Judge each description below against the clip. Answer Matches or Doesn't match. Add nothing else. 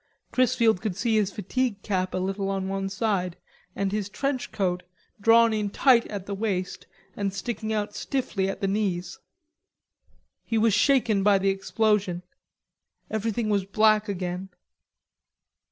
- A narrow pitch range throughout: Matches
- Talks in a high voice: Matches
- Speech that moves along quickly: Doesn't match